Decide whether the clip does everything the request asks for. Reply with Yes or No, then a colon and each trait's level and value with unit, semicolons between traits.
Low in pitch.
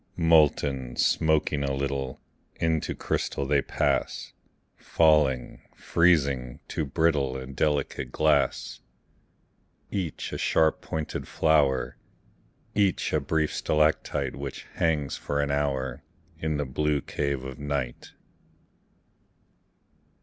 Yes: very low, 70 Hz